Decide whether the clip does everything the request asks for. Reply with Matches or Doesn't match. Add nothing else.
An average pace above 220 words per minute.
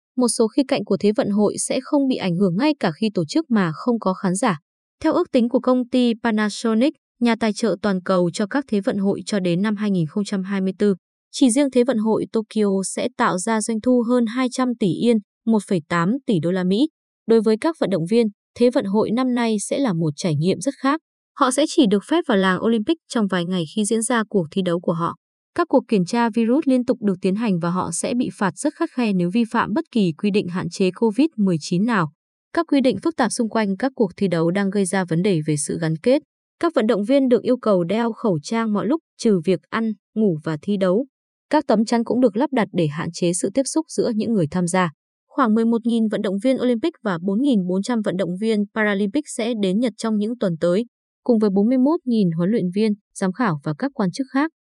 Matches